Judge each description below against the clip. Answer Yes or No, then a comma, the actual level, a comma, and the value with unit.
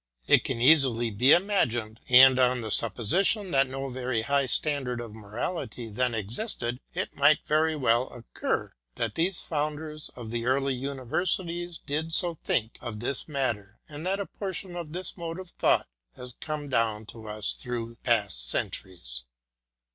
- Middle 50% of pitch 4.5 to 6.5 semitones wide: Yes, average, 5.2 semitones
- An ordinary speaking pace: Yes, average, 165 wpm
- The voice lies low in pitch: Yes, low, 130 Hz